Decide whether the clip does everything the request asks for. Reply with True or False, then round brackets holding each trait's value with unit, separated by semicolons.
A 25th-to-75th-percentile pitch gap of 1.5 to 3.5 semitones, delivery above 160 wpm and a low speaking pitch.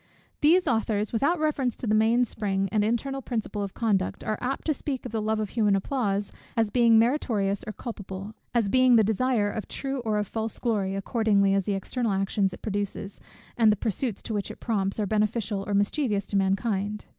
False (3.0 semitones; 200 wpm; 215 Hz)